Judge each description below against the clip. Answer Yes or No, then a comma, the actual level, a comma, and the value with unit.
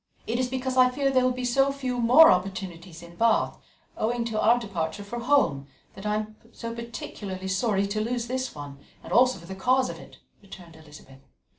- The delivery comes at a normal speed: Yes, average, 195 wpm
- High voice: Yes, high, 225 Hz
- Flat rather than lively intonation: No, average, 4.9 semitones